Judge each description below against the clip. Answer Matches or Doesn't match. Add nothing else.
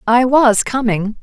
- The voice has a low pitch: Doesn't match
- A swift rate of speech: Doesn't match